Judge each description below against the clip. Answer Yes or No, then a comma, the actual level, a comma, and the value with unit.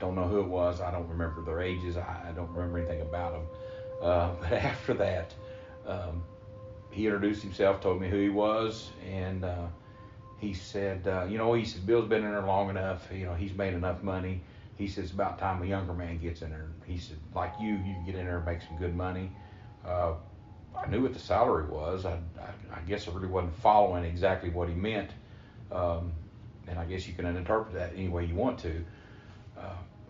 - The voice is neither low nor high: No, very low, 95 Hz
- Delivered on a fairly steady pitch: No, average, 3.1 semitones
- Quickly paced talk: Yes, fast, 215 wpm